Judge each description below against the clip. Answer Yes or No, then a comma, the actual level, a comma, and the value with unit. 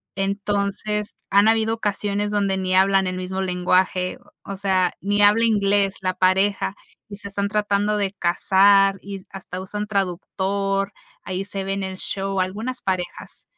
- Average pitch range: No, narrow, 1.3 semitones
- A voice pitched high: Yes, high, 195 Hz